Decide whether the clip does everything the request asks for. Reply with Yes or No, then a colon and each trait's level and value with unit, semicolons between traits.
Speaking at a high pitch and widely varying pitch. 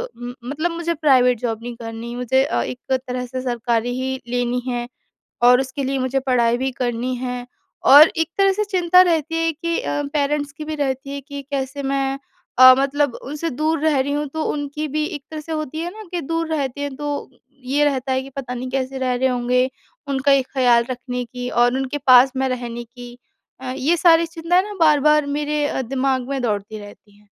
No: very high, 265 Hz; average, 3.2 semitones